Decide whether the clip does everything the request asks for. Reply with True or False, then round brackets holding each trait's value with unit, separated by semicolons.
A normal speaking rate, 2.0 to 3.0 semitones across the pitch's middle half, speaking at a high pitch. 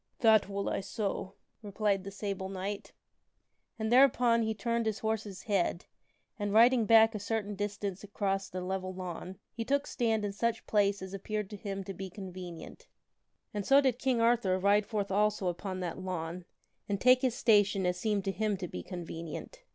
True (185 wpm; 2.7 semitones; 205 Hz)